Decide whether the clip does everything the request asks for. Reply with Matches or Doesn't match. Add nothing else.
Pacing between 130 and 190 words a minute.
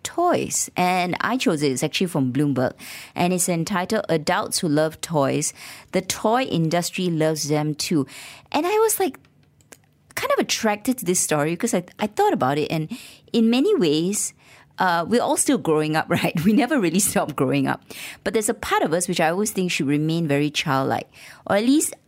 Doesn't match